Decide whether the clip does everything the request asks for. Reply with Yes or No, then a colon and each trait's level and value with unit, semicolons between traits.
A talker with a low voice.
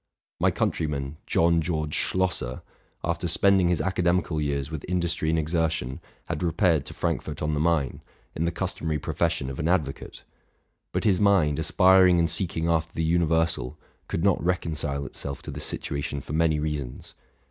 Yes: very low, 80 Hz